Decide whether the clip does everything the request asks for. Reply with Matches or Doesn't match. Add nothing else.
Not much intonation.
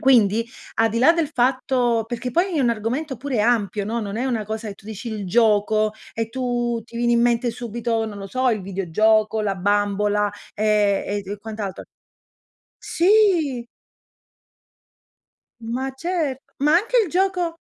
Doesn't match